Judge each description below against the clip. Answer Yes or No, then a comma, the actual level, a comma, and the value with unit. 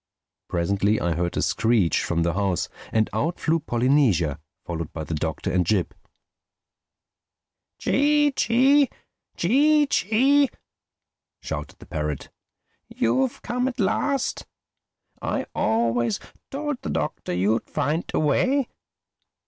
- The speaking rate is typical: No, slow, 115 wpm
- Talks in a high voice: No, low, 120 Hz